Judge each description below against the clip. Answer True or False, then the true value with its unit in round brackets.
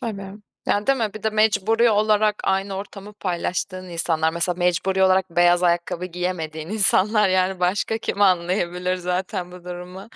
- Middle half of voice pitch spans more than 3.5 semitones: False (2.5 semitones)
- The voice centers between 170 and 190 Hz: True (185 Hz)